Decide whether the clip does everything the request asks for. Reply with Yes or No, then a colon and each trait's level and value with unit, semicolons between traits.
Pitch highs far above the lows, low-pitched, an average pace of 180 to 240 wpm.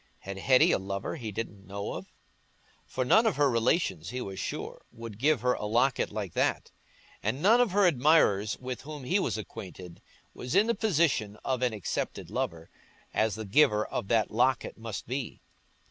Yes: wide, 5.7 semitones; low, 120 Hz; average, 185 wpm